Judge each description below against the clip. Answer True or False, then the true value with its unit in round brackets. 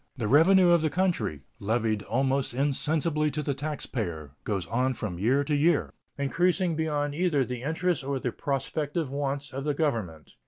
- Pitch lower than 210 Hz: True (140 Hz)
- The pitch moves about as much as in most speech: True (4.2 semitones)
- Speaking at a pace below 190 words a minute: True (165 wpm)